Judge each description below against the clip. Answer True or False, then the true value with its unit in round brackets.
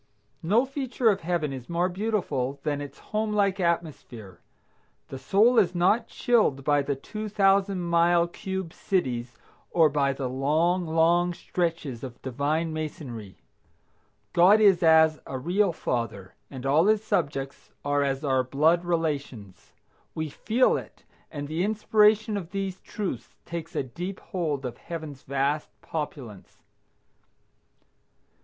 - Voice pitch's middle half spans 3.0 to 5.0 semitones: False (5.6 semitones)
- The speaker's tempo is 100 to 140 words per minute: True (135 wpm)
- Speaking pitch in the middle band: True (165 Hz)